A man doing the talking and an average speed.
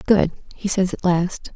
No: female; average, 195 wpm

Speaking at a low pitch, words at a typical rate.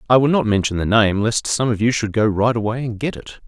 No: low, 115 Hz; fast, 295 wpm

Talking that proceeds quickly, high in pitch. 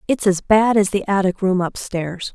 Yes: fast, 230 wpm; high, 195 Hz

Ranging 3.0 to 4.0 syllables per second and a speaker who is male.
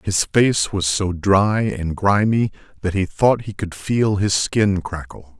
Yes: 3.6 syllables/s; male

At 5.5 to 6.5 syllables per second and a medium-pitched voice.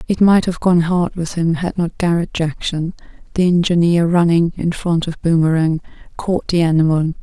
No: 4.9 syllables/s; medium, 170 Hz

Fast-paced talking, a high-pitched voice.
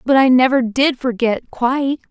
No: average, 140 wpm; very high, 255 Hz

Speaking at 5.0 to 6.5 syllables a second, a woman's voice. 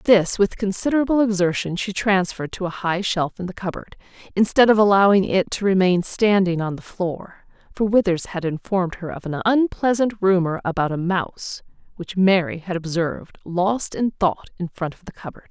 Yes: 5.3 syllables/s; female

